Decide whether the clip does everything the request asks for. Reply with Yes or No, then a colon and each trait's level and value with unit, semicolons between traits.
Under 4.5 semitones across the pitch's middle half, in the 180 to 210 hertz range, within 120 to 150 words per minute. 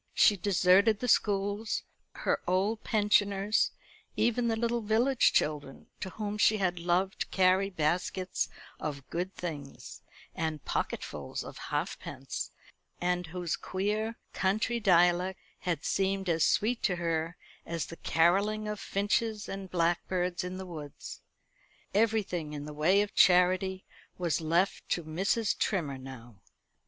Yes: average, 3.5 semitones; medium, 185 Hz; slow, 135 wpm